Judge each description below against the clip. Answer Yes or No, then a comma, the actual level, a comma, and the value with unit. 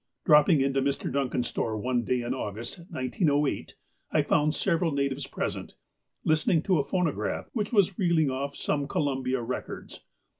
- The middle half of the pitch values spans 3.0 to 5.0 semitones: Yes, average, 3.8 semitones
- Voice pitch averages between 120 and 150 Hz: Yes, medium, 140 Hz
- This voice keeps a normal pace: Yes, average, 155 wpm